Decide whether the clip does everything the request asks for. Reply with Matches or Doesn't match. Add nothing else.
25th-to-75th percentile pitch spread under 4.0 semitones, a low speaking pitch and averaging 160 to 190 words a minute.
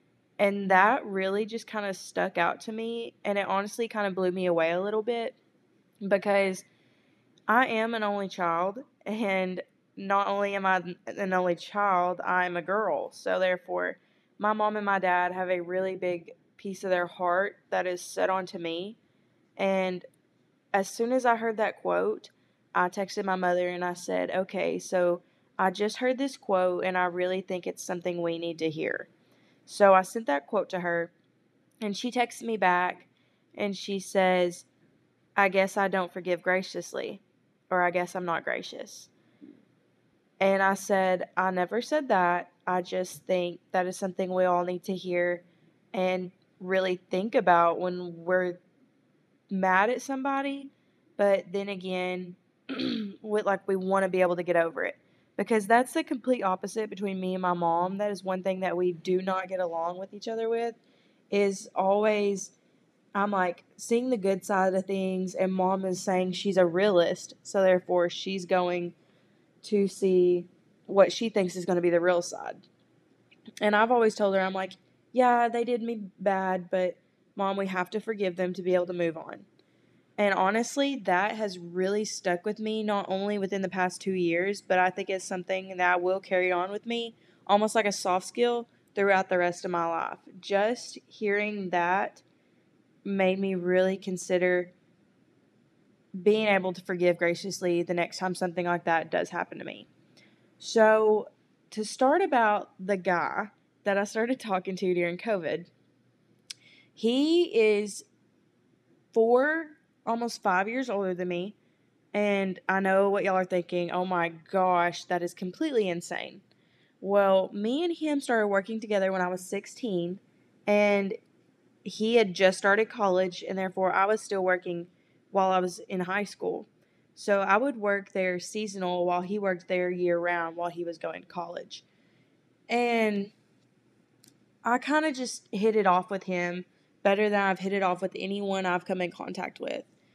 Doesn't match